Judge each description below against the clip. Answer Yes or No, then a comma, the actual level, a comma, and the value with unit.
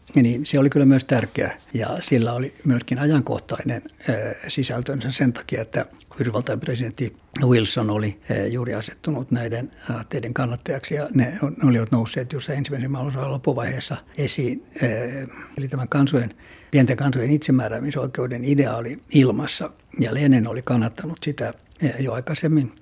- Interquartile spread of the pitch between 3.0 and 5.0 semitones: No, narrow, 2.6 semitones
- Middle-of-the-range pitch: No, low, 130 Hz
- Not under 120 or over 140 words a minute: Yes, average, 130 wpm